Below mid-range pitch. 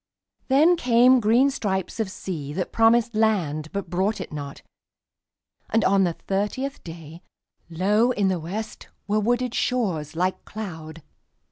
No: high, 200 Hz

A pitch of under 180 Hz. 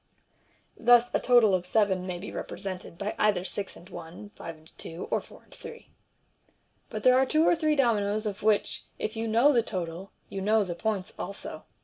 No: high, 205 Hz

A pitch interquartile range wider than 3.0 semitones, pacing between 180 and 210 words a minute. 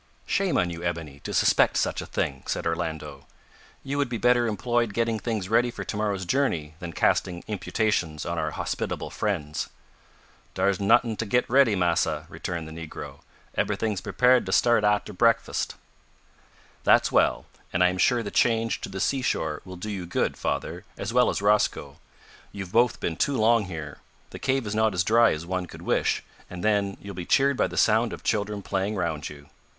Yes: average, 4.9 semitones; average, 190 wpm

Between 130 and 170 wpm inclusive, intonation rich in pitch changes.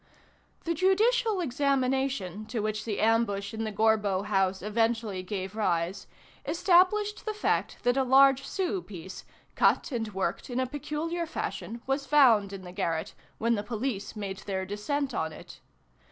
Yes: average, 155 wpm; wide, 5.7 semitones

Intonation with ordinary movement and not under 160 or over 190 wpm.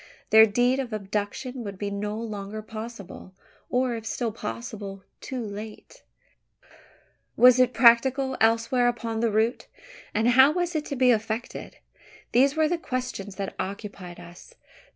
No: average, 3.5 semitones; average, 150 wpm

